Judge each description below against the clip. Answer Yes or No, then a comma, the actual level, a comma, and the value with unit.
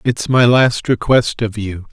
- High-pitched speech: No, low, 115 Hz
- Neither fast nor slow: Yes, average, 190 wpm